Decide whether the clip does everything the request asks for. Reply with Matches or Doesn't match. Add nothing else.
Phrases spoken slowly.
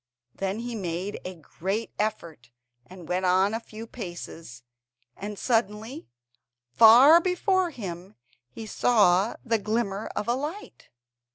Matches